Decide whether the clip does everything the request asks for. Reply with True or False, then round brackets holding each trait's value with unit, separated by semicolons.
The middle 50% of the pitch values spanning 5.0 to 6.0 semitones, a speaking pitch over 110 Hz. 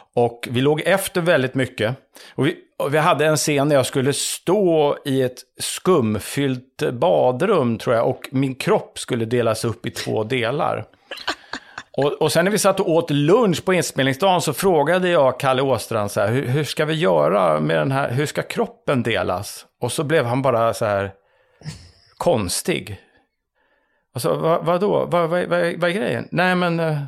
True (5.6 semitones; 140 Hz)